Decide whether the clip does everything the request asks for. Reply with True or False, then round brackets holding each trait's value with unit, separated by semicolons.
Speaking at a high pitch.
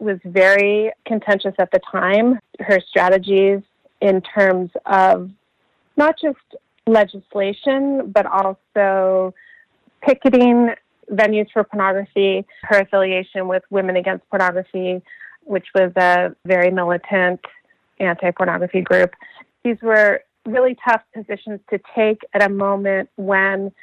True (195 Hz)